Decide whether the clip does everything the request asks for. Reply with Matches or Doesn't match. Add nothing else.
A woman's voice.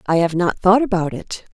Matches